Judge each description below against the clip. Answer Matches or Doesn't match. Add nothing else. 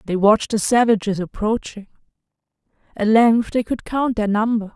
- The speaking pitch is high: Matches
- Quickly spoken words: Doesn't match